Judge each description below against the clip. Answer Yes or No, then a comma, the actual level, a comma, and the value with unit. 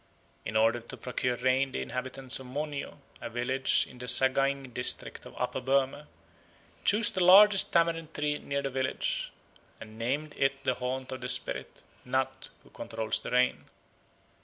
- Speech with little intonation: Yes, narrow, 2.1 semitones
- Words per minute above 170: No, average, 160 wpm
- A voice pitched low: Yes, low, 130 Hz